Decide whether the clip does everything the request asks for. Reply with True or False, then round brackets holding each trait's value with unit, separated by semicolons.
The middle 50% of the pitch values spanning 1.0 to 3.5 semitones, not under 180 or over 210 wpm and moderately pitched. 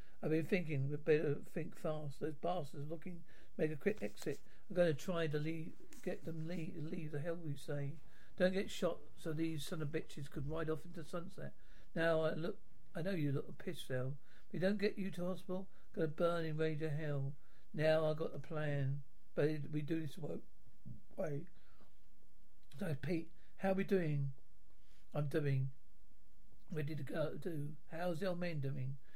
True (3.0 semitones; 190 wpm; 160 Hz)